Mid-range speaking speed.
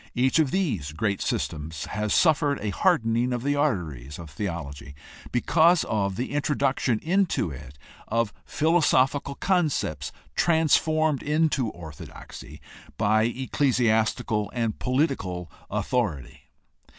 No: slow, 110 wpm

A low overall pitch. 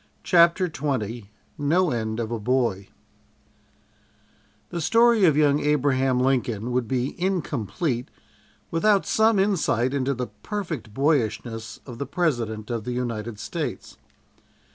Yes: low, 130 Hz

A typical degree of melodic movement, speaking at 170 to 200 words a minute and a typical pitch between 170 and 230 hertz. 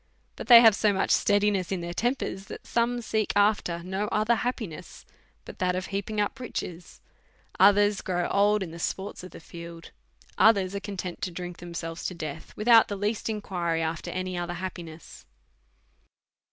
Yes: average, 3.2 semitones; average, 175 wpm; high, 190 Hz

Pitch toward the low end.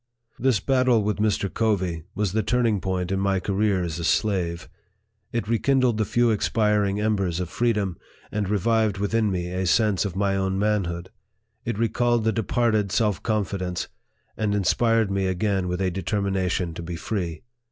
Yes: low, 100 Hz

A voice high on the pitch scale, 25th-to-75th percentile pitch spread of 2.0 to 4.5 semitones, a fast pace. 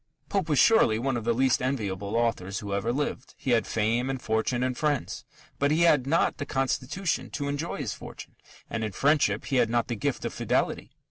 No: low, 125 Hz; average, 4.0 semitones; fast, 210 wpm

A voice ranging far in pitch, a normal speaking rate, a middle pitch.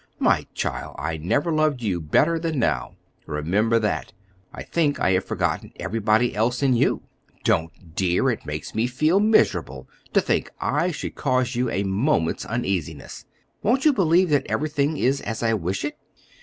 No: wide, 8.3 semitones; average, 170 wpm; low, 120 Hz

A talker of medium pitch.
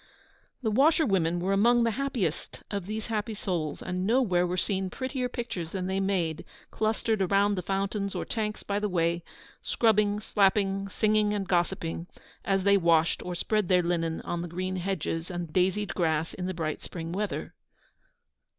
No: high, 195 Hz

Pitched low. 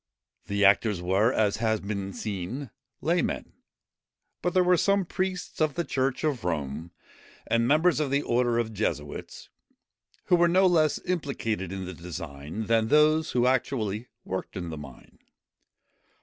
Yes: low, 115 Hz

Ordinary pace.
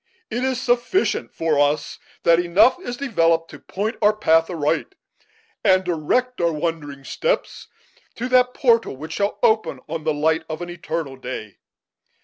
Yes: average, 160 wpm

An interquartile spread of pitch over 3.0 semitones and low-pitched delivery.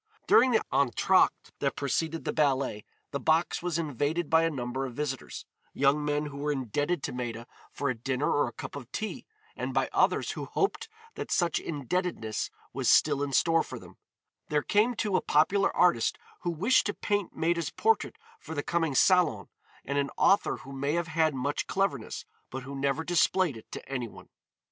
No: average, 4.1 semitones; medium, 150 Hz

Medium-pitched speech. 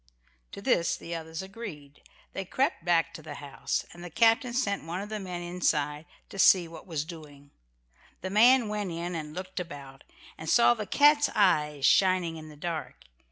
Yes: medium, 175 Hz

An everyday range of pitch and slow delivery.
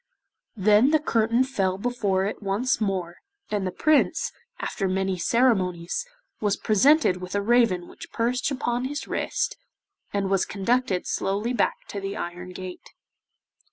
No: average, 4.5 semitones; average, 145 wpm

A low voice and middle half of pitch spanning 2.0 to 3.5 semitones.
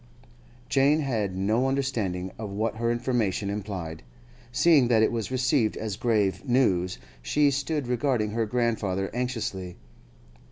No: low, 115 Hz; average, 4.6 semitones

